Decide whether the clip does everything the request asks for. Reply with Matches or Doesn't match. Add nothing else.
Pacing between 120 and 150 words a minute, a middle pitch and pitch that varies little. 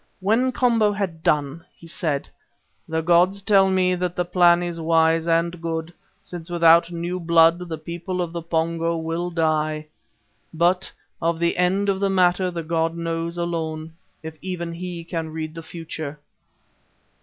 Doesn't match